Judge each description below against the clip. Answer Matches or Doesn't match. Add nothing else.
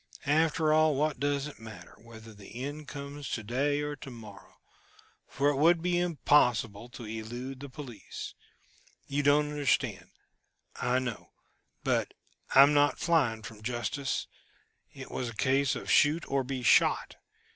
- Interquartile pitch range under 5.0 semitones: Matches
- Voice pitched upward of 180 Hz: Doesn't match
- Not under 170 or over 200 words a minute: Doesn't match